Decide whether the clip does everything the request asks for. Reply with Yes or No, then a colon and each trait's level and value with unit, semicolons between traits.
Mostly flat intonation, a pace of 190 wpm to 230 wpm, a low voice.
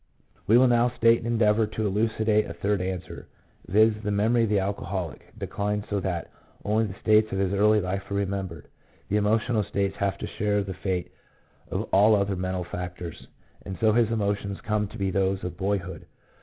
Yes: narrow, 2.2 semitones; average, 195 wpm; low, 100 Hz